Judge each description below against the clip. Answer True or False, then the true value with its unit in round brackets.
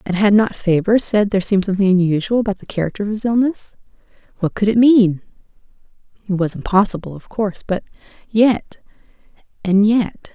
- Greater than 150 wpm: False (140 wpm)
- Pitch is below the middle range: False (200 Hz)